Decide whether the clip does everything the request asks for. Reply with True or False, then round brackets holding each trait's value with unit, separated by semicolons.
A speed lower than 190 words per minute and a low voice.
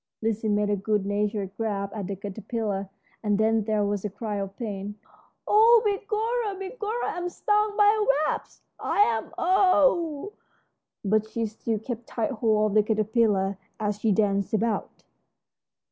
False (155 wpm; 220 Hz)